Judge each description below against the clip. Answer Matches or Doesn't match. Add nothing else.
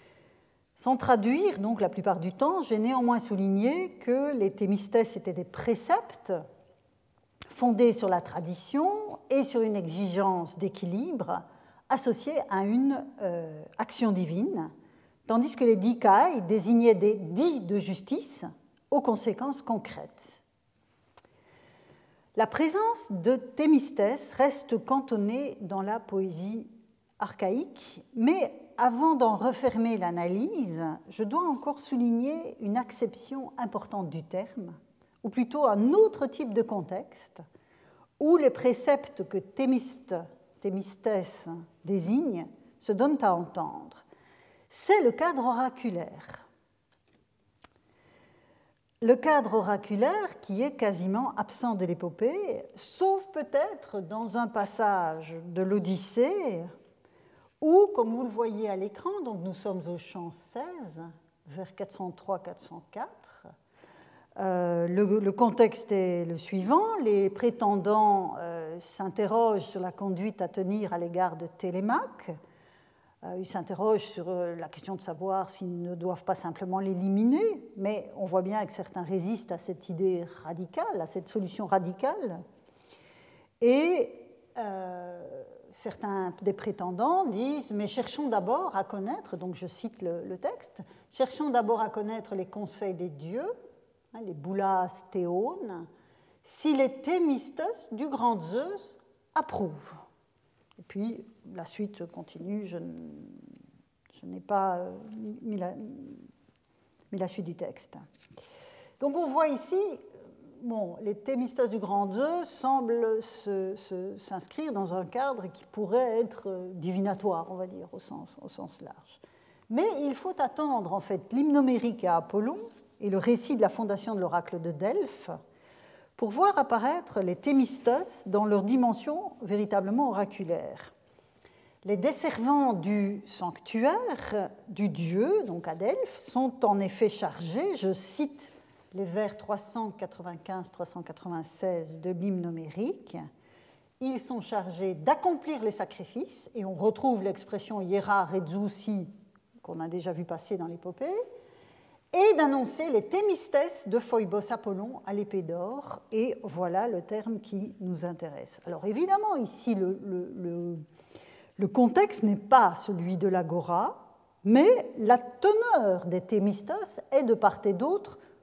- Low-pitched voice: Doesn't match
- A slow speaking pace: Matches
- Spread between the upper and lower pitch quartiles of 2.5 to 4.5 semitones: Doesn't match